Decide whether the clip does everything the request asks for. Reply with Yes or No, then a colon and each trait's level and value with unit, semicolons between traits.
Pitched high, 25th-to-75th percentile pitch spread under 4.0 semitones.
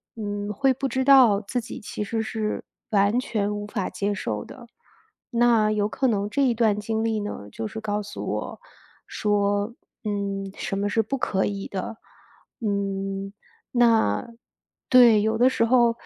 Yes: high, 210 Hz; narrow, 2.5 semitones